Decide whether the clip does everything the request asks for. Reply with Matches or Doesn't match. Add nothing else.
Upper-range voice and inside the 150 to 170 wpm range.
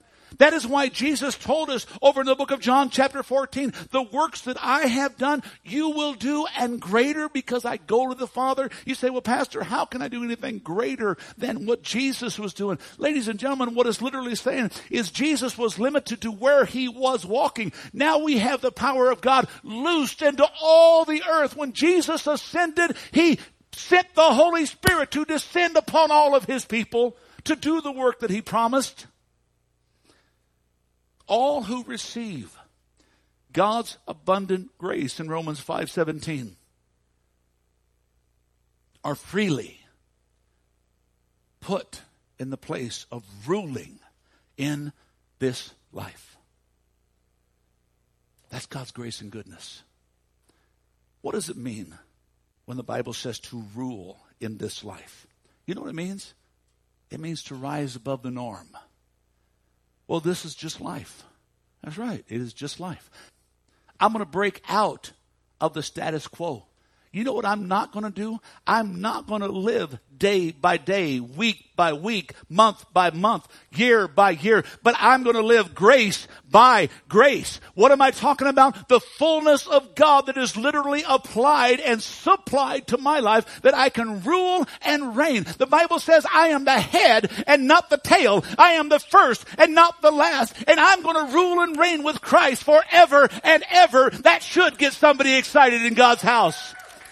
Matches